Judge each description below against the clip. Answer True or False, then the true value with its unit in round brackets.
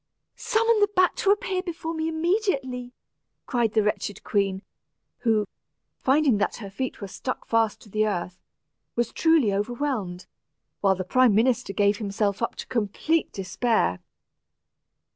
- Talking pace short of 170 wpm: True (145 wpm)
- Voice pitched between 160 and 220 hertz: False (230 Hz)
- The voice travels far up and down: True (7.4 semitones)